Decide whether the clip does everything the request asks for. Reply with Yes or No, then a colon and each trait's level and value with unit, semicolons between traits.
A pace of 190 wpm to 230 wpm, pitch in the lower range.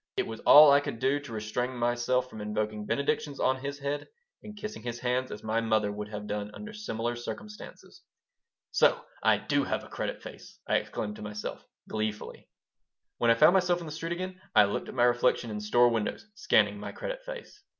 Yes: average, 200 wpm; low, 120 Hz